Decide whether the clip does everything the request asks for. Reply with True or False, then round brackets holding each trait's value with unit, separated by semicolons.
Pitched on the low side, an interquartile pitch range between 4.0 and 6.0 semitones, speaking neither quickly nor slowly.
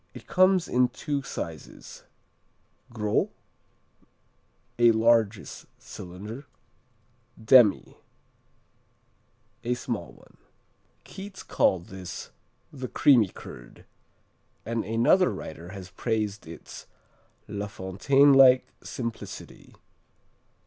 False (115 Hz; 4.9 semitones; 85 wpm)